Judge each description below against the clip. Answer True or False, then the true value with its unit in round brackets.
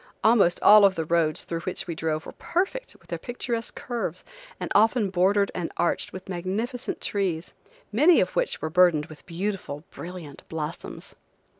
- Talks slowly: False (165 wpm)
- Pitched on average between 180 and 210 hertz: True (185 Hz)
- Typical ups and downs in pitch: True (4.9 semitones)